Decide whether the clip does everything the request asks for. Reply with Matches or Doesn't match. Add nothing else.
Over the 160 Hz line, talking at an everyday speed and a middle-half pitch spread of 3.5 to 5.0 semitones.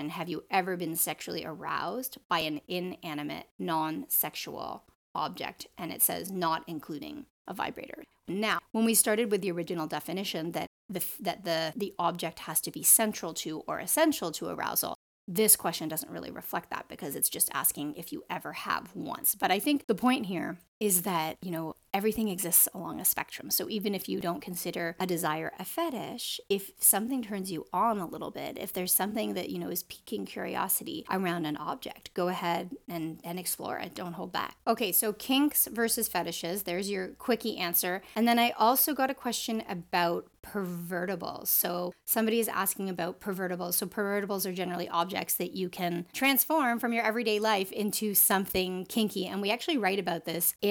Matches